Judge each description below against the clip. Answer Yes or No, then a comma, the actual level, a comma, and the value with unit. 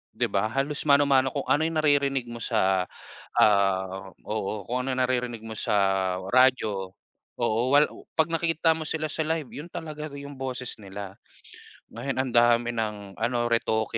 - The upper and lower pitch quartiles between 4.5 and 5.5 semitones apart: Yes, average, 4.8 semitones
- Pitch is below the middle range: Yes, low, 125 Hz